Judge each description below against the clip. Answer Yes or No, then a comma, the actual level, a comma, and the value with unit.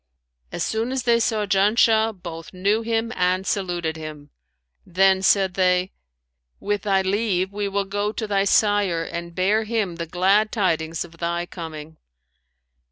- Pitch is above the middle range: Yes, high, 195 Hz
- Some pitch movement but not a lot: Yes, average, 3.4 semitones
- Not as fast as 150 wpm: No, average, 155 wpm